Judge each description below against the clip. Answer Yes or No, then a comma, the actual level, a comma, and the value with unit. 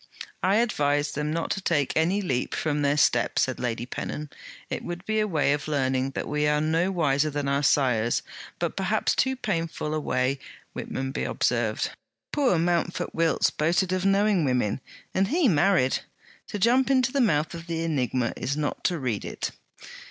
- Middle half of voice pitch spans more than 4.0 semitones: Yes, average, 5.0 semitones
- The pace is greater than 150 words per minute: Yes, average, 180 wpm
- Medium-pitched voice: Yes, medium, 155 Hz